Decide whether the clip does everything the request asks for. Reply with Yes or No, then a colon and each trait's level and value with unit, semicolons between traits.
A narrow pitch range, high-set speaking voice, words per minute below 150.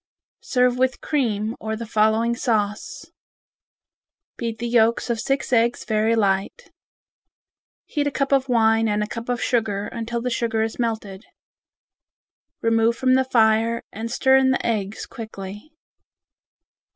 Yes: narrow, 2.1 semitones; high, 230 Hz; average, 140 wpm